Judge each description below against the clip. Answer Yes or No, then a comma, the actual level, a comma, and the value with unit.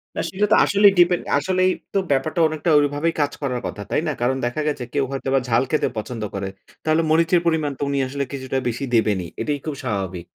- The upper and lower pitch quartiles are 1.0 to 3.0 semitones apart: No, average, 4.8 semitones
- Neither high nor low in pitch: Yes, medium, 145 Hz